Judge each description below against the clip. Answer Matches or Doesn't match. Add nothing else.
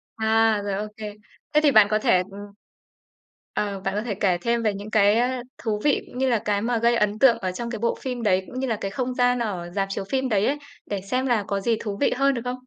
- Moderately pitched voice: Doesn't match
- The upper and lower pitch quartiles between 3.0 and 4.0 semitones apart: Matches